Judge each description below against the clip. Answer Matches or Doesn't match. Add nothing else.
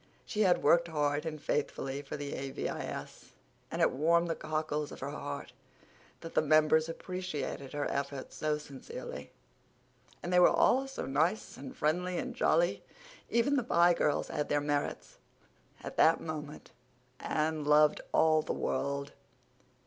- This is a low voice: Doesn't match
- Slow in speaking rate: Doesn't match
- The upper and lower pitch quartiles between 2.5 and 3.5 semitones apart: Matches